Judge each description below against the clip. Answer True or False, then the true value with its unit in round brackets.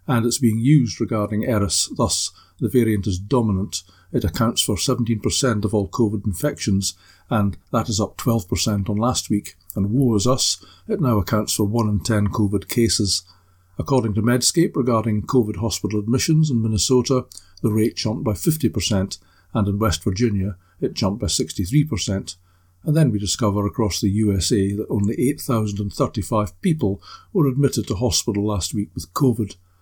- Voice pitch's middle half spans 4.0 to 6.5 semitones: False (3.4 semitones)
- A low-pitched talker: True (105 Hz)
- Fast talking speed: False (165 wpm)